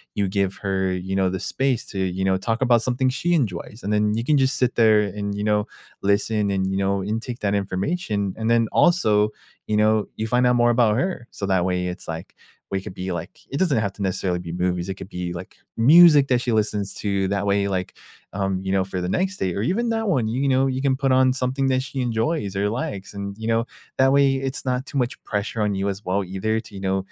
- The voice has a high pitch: No, low, 105 Hz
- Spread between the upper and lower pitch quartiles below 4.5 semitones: No, average, 4.8 semitones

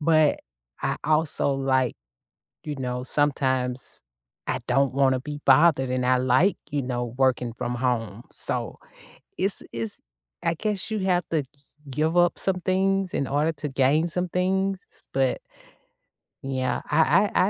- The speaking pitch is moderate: Yes, medium, 145 Hz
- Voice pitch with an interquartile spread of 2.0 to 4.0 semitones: No, average, 5.0 semitones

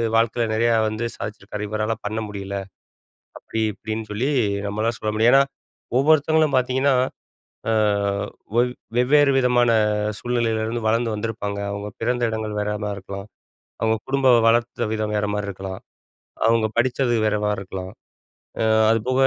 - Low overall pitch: Yes, low, 110 Hz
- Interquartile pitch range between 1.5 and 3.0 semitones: Yes, narrow, 2.6 semitones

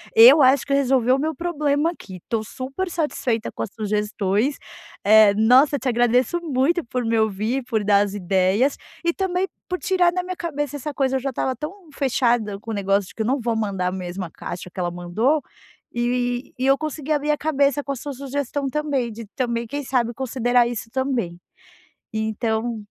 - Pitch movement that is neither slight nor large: Yes, average, 4.7 semitones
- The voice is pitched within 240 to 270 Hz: Yes, very high, 250 Hz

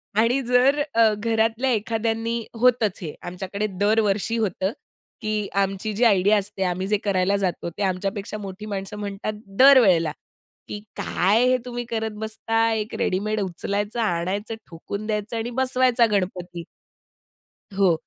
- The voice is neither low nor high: No, high, 210 Hz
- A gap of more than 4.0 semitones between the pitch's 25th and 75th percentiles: No, average, 2.7 semitones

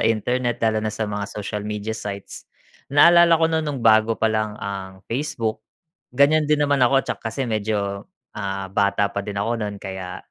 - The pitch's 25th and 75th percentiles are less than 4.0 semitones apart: No, average, 4.6 semitones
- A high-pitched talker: No, low, 110 Hz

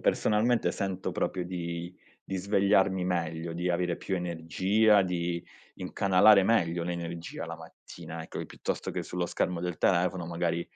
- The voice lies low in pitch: Yes, very low, 90 Hz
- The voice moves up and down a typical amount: No, narrow, 2.0 semitones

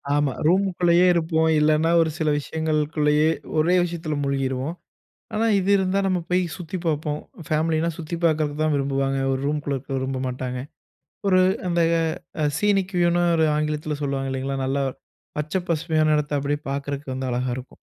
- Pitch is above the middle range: No, medium, 155 Hz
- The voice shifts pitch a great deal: No, average, 3.4 semitones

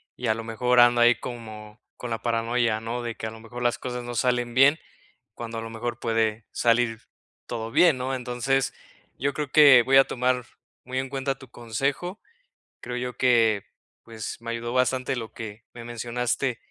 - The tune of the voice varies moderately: No, narrow, 1.9 semitones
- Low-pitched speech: Yes, low, 120 Hz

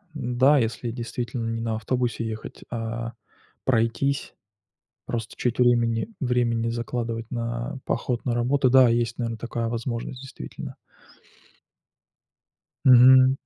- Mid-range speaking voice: No, low, 120 Hz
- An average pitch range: No, narrow, 1.5 semitones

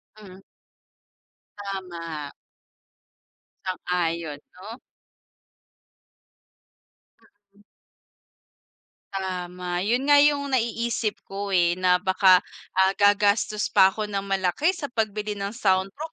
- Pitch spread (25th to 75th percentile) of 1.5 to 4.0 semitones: Yes, average, 2.9 semitones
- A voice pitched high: Yes, high, 195 Hz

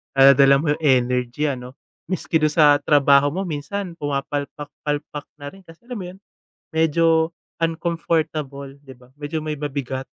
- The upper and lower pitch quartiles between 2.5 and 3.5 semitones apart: Yes, average, 2.8 semitones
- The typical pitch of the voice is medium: Yes, medium, 145 Hz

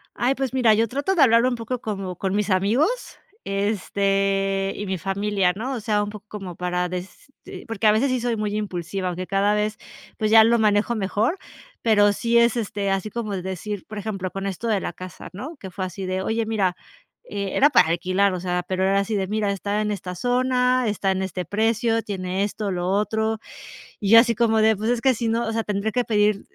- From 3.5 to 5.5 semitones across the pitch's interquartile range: No, average, 2.9 semitones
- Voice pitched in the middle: No, high, 210 Hz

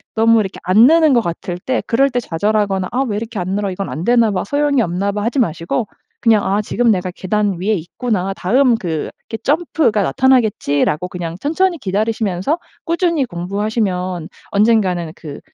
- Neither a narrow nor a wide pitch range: Yes, average, 4.9 semitones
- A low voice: No, high, 210 Hz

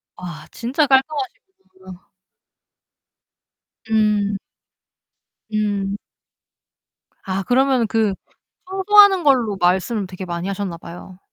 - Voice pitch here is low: No, high, 210 Hz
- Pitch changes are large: Yes, wide, 6.1 semitones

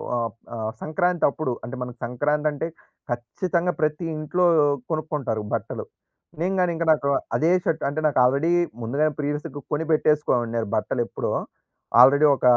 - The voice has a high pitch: No, medium, 150 Hz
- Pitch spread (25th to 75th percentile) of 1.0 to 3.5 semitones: No, average, 4.1 semitones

